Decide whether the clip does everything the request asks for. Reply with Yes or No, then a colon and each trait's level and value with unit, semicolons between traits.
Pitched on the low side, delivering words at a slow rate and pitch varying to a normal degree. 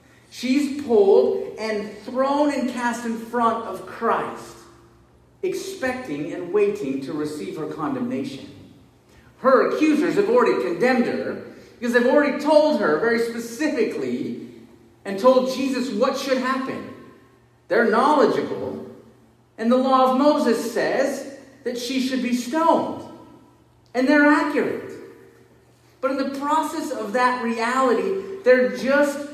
No: very high, 265 Hz; slow, 125 wpm; average, 4.2 semitones